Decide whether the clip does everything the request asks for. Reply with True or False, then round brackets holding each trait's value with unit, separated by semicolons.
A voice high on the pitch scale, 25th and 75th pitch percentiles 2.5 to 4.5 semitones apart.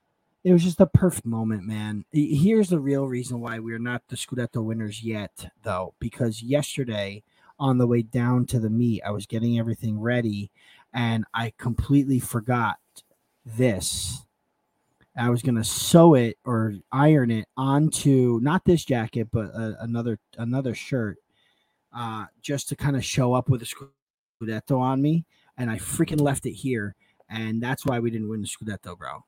False (120 Hz; 3.6 semitones)